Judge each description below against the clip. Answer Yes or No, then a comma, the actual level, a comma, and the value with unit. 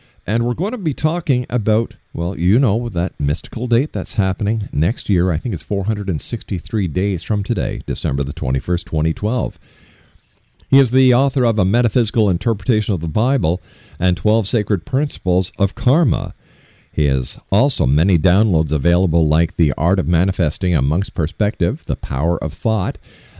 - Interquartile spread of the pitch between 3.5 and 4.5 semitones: No, wide, 5.6 semitones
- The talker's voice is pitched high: No, low, 100 Hz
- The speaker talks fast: No, average, 160 wpm